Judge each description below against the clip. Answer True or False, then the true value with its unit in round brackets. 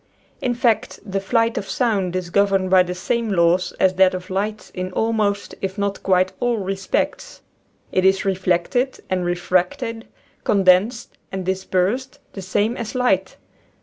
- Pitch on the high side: True (195 Hz)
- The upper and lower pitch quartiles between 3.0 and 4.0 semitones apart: True (3.4 semitones)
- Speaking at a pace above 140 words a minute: True (155 wpm)